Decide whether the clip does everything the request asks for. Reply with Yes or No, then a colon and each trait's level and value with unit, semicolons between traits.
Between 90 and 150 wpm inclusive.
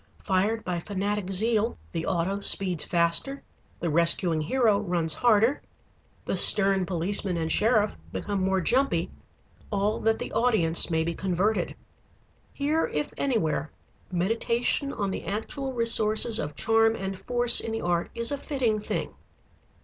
Yes: average, 140 wpm